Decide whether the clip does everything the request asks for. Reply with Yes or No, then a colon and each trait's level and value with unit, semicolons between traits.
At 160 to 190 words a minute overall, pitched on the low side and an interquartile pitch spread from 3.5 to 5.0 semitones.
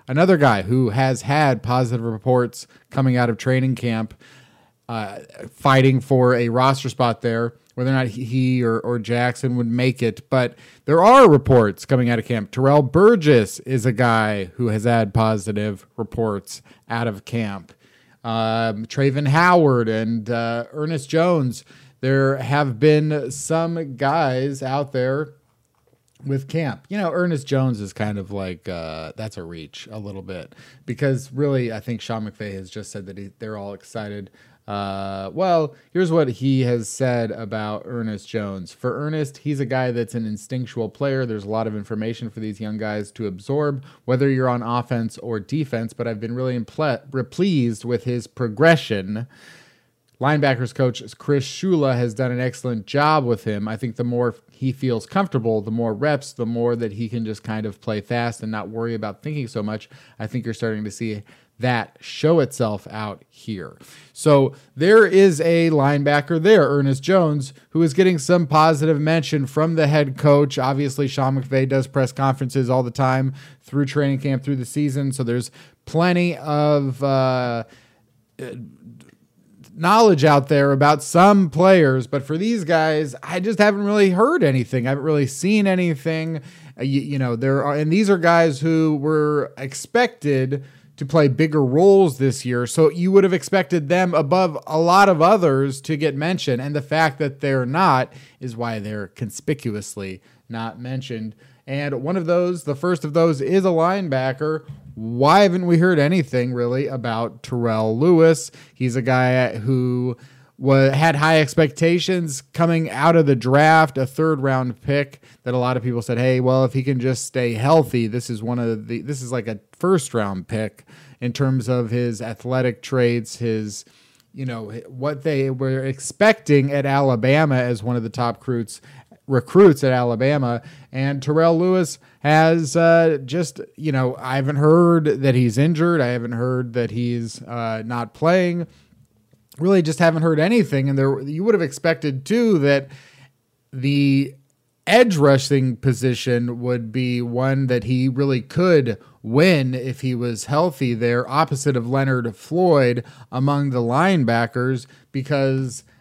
Yes: average, 170 wpm; low, 130 Hz; average, 4.1 semitones